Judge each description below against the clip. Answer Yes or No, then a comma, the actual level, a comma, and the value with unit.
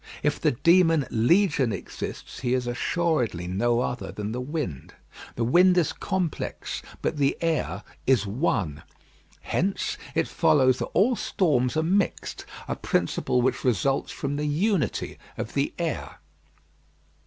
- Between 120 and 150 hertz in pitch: Yes, low, 135 Hz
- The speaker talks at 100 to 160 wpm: Yes, average, 140 wpm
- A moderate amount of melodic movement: No, wide, 5.9 semitones